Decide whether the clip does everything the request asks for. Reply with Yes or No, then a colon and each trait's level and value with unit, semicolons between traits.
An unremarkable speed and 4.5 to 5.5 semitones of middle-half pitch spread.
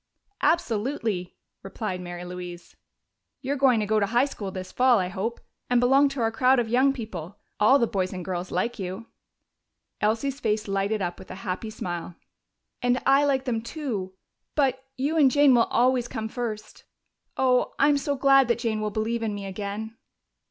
Yes: average, 180 wpm; average, 5.0 semitones